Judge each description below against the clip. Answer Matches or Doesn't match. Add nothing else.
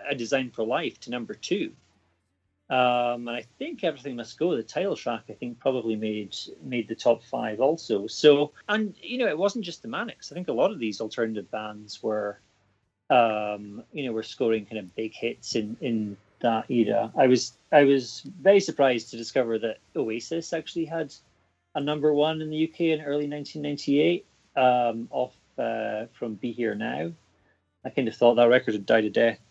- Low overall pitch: Matches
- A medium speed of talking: Matches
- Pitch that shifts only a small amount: Doesn't match